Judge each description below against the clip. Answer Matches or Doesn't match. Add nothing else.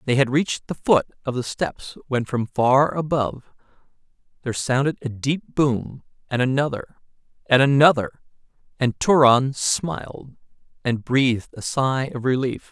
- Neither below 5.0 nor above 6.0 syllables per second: Doesn't match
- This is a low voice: Matches